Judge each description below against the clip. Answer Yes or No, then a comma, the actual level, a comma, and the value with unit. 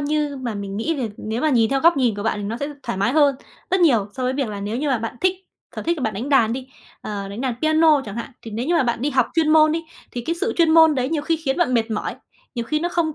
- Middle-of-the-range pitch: No, very high, 265 Hz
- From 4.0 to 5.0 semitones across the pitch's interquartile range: No, wide, 5.6 semitones